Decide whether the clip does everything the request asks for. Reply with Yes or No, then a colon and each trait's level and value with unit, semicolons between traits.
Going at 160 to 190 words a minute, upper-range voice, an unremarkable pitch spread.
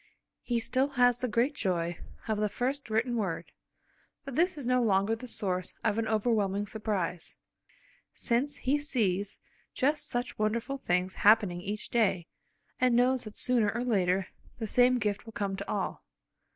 Yes: average, 165 wpm; high, 225 Hz; average, 3.8 semitones